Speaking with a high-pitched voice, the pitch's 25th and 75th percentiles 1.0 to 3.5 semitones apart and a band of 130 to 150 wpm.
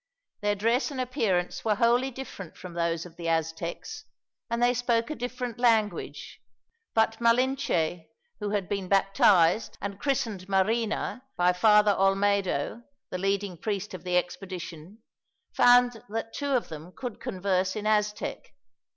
No: high, 205 Hz; average, 4.4 semitones; average, 140 wpm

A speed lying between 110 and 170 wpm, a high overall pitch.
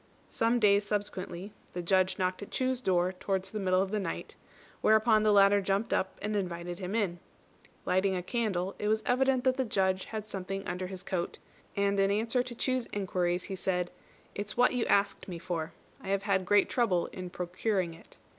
No: average, 195 wpm; high, 195 Hz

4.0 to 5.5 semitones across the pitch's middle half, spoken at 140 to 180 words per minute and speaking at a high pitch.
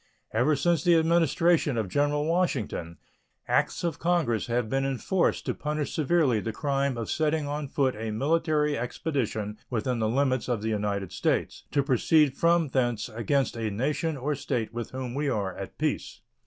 No: average, 5.0 semitones; average, 170 wpm; low, 135 Hz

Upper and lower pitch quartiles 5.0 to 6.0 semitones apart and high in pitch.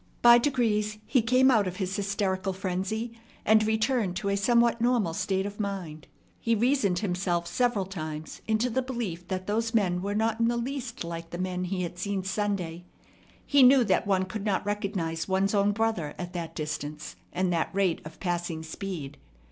No: average, 4.0 semitones; high, 200 Hz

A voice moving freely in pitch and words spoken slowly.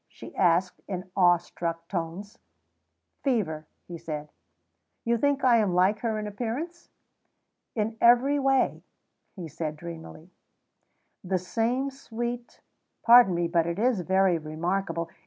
Yes: wide, 5.7 semitones; slow, 130 wpm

